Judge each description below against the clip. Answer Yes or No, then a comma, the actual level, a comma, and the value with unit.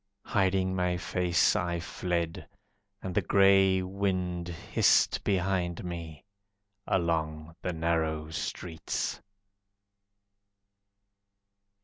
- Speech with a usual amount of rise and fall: No, narrow, 2.1 semitones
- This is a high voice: No, very low, 90 Hz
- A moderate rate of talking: No, slow, 80 wpm